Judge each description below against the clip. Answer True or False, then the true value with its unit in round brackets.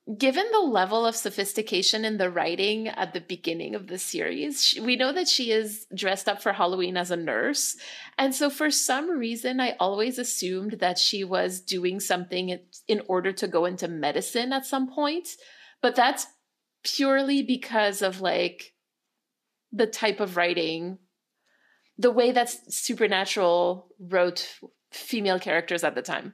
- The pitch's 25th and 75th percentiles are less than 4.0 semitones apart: False (5.6 semitones)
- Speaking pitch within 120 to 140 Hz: False (210 Hz)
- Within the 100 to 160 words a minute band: True (155 wpm)